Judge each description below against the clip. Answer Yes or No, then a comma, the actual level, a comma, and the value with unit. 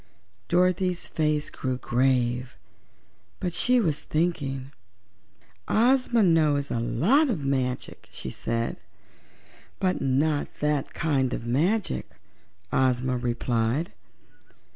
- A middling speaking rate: No, slow, 100 wpm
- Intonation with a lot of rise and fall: Yes, wide, 5.7 semitones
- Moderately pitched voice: Yes, medium, 145 Hz